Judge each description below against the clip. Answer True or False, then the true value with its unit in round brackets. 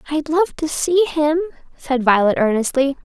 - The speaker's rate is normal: True (150 wpm)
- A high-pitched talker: True (295 Hz)